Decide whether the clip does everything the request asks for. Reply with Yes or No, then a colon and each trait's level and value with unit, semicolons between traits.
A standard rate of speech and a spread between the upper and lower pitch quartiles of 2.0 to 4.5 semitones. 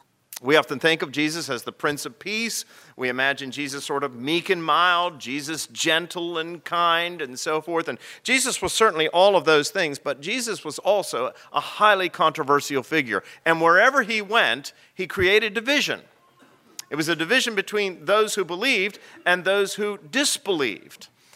No: average, 170 wpm; average, 5.3 semitones